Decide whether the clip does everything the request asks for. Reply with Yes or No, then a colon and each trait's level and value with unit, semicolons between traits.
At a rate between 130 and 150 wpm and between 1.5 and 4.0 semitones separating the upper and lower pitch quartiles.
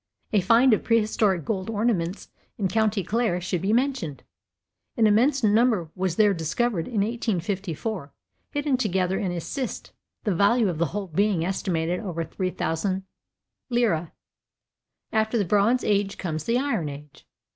No: average, 145 wpm; average, 4.4 semitones